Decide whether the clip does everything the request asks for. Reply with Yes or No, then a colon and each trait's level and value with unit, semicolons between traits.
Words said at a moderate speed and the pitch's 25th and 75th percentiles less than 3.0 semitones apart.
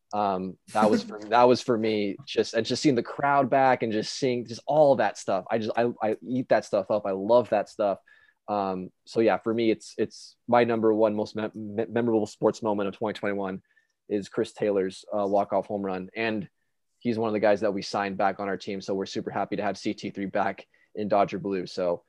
No: fast, 235 wpm; narrow, 2.4 semitones